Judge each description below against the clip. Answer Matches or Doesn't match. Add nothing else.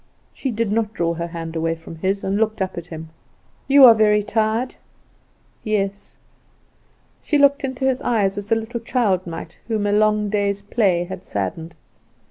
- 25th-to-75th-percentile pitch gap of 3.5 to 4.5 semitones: Matches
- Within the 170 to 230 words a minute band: Matches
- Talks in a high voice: Matches